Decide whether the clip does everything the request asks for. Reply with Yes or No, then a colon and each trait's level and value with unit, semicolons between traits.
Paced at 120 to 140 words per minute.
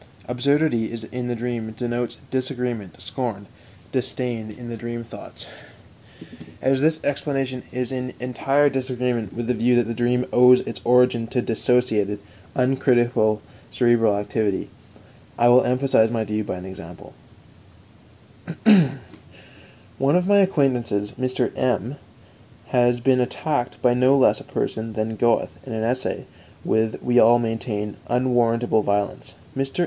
Yes: slow, 135 wpm